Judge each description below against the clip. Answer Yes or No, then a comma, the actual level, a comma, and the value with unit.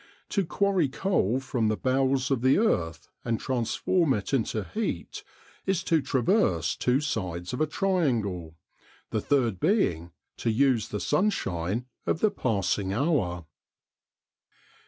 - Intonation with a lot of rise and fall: Yes, wide, 7.5 semitones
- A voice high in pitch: No, low, 125 Hz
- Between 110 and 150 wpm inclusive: Yes, slow, 135 wpm